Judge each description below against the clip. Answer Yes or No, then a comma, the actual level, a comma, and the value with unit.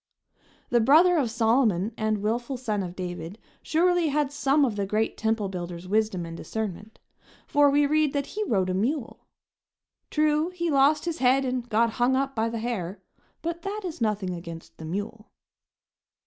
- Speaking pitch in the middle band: No, high, 235 Hz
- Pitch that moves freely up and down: Yes, wide, 6.2 semitones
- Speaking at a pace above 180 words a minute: No, average, 175 wpm